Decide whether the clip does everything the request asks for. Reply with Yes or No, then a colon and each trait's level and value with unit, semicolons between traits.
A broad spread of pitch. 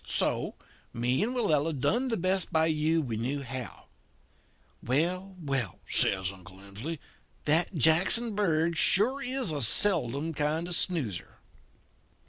Yes: wide, 6.2 semitones